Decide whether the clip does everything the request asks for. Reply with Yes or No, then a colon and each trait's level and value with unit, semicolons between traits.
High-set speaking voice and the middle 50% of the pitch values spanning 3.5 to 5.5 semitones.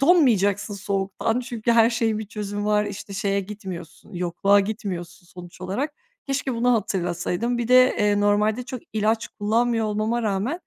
No: high, 210 Hz; average, 3.0 semitones